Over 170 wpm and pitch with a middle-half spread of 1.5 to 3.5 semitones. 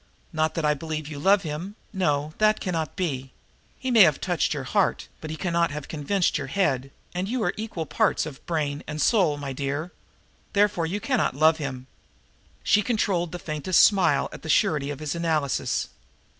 No: average, 190 wpm; average, 4.2 semitones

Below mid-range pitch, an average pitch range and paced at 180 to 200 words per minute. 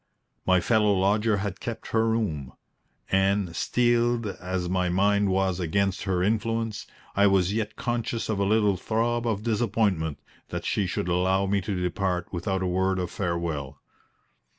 No: low, 100 Hz; average, 3.2 semitones; average, 155 wpm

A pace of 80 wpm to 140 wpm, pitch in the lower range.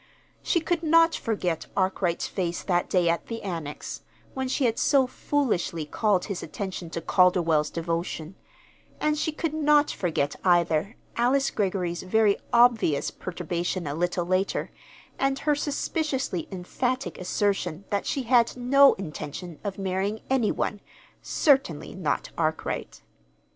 No: slow, 135 wpm; high, 195 Hz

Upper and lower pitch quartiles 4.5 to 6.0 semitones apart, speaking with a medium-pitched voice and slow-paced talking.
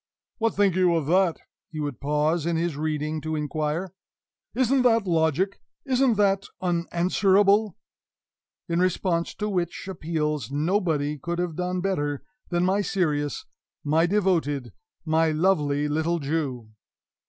No: average, 3.9 semitones; medium, 170 Hz; slow, 130 wpm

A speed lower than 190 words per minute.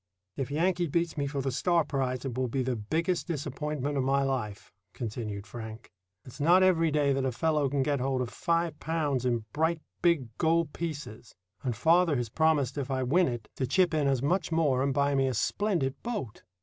No: fast, 205 wpm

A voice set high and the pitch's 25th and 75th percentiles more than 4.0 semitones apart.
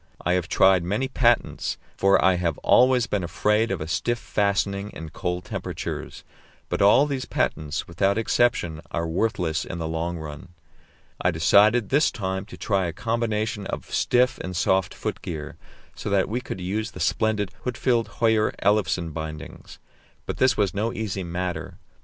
No: low, 100 Hz; average, 4.4 semitones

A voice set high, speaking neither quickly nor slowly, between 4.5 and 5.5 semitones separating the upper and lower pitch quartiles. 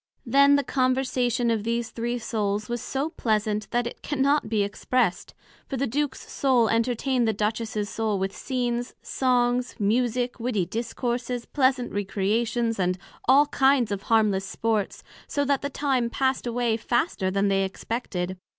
No: high, 235 Hz; average, 150 wpm; average, 3.3 semitones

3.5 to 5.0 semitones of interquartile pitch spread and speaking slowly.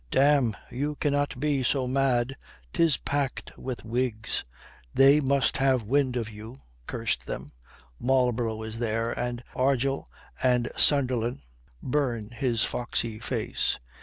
No: average, 2.8 semitones; slow, 125 wpm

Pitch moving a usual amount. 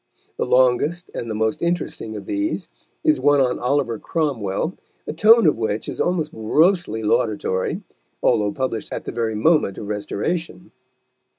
No: wide, 7.6 semitones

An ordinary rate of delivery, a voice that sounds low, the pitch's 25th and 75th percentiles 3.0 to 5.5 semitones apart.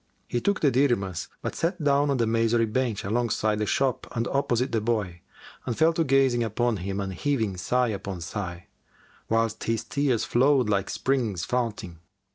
Yes: average, 175 wpm; low, 115 Hz; average, 4.3 semitones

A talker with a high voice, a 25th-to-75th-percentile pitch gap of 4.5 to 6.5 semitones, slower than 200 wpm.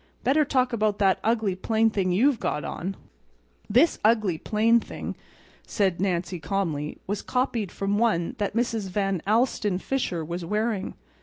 No: high, 205 Hz; average, 3.8 semitones; average, 150 wpm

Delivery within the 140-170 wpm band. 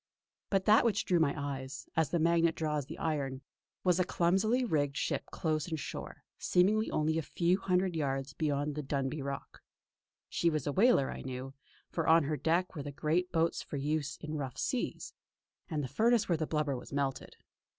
No: average, 190 wpm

